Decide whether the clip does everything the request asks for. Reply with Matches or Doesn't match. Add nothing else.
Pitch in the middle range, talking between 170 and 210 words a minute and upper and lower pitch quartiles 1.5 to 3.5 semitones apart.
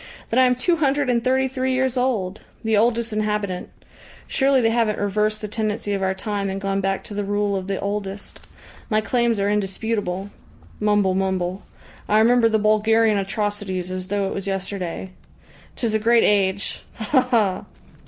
Doesn't match